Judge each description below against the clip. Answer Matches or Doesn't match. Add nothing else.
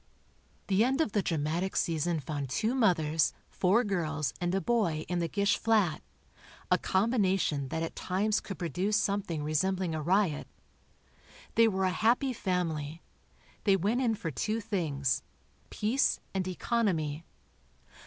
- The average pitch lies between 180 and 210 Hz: Matches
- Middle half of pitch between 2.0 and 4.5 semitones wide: Doesn't match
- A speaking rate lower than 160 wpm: Matches